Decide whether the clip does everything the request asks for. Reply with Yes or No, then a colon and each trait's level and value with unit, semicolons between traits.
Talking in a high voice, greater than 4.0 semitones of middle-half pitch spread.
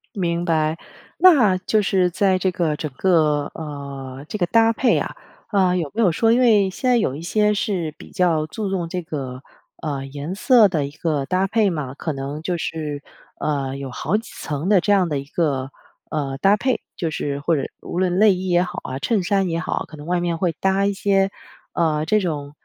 No: medium, 175 Hz; average, 4.7 semitones